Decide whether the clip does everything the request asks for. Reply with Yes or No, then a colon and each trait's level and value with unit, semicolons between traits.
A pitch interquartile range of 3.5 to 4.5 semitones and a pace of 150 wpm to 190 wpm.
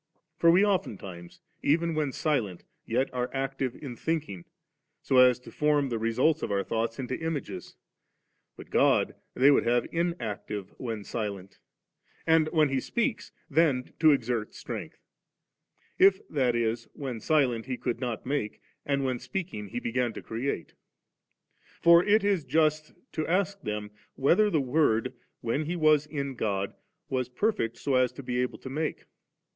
No: average, 5.1 semitones; average, 160 wpm